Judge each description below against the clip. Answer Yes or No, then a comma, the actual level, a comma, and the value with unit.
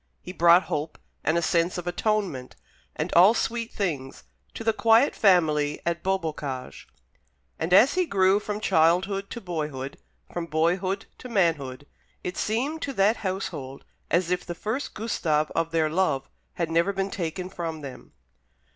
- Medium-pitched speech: Yes, medium, 175 Hz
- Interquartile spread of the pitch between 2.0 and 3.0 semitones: No, average, 4.0 semitones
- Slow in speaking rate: No, average, 155 wpm